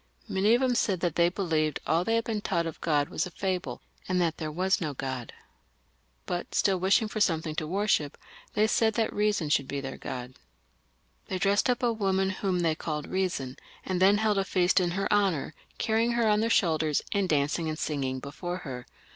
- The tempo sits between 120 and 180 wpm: No, fast, 205 wpm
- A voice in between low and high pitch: Yes, medium, 180 Hz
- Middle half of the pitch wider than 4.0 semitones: Yes, average, 4.9 semitones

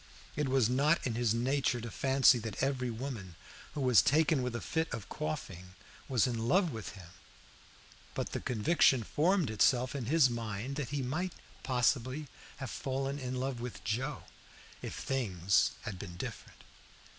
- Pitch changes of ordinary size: Yes, average, 3.5 semitones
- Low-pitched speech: Yes, low, 125 Hz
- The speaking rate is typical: Yes, average, 165 wpm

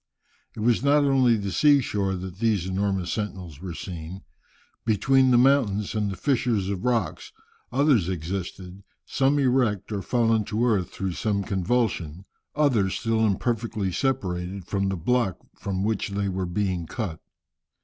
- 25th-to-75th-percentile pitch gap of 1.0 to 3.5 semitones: No, average, 4.4 semitones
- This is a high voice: No, low, 100 Hz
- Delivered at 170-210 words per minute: No, average, 155 wpm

